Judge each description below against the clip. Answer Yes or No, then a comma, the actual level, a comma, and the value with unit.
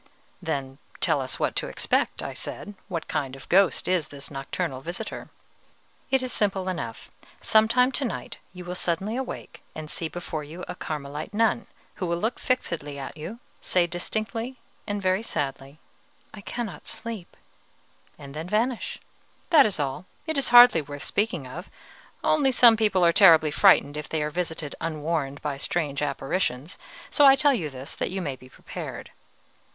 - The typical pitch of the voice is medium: Yes, medium, 175 Hz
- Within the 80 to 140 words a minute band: No, average, 175 wpm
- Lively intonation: Yes, wide, 6.8 semitones